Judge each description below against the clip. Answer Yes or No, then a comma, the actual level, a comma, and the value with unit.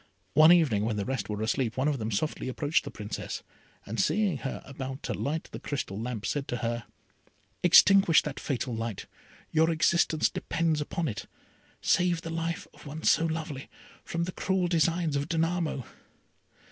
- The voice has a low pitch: No, medium, 150 Hz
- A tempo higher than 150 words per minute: Yes, average, 170 wpm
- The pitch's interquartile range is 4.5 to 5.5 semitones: Yes, average, 5.1 semitones